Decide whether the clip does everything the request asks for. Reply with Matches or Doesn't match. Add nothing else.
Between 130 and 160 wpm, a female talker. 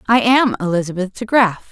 Matches